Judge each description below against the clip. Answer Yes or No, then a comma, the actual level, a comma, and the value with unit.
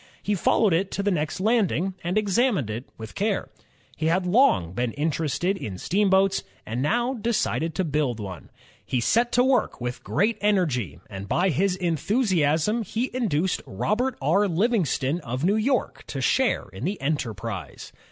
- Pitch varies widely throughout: Yes, wide, 7.5 semitones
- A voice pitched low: No, medium, 180 Hz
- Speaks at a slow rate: No, average, 165 wpm